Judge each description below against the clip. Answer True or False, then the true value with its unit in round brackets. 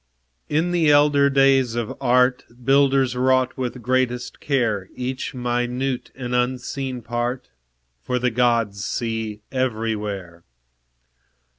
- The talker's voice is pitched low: True (125 Hz)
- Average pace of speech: False (110 wpm)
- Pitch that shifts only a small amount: True (2.0 semitones)